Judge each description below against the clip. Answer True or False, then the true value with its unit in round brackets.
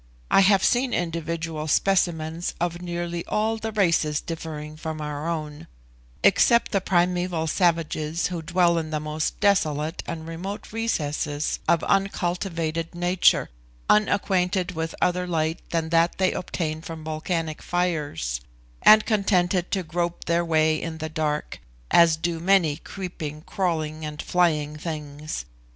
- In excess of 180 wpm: False (135 wpm)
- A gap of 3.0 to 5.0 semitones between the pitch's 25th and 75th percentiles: False (2.5 semitones)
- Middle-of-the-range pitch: True (165 Hz)